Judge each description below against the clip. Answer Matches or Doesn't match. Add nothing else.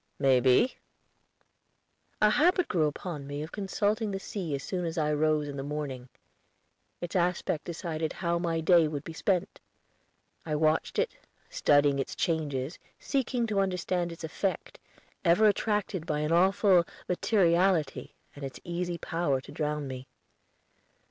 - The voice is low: Doesn't match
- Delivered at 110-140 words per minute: Doesn't match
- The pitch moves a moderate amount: Matches